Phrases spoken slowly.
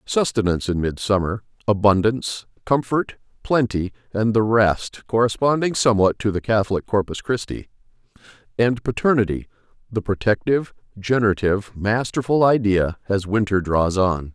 Yes: slow, 115 wpm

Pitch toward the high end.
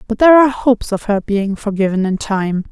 Yes: high, 215 Hz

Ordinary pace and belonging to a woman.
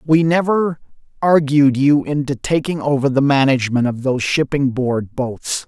No: average, 150 wpm; male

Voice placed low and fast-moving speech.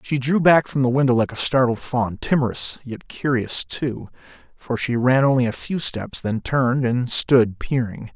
No: low, 125 Hz; average, 190 wpm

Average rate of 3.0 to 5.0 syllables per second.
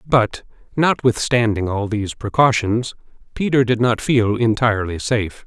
Yes: 4.7 syllables/s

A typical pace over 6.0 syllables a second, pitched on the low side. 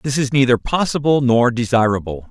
No: 5.3 syllables/s; low, 125 Hz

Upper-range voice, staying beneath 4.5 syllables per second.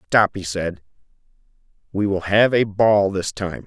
No: low, 100 Hz; 4.1 syllables/s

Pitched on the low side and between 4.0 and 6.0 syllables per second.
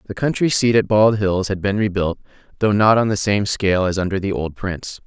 Yes: low, 100 Hz; 5.6 syllables/s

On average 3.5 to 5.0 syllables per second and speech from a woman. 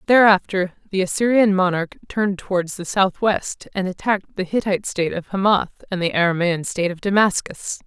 No: 5.5 syllables/s; female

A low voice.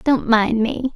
No: high, 240 Hz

